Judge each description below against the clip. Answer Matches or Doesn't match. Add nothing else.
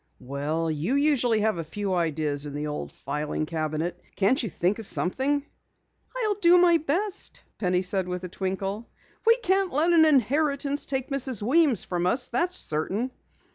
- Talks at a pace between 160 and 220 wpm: Matches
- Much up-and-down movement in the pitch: Matches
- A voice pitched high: Matches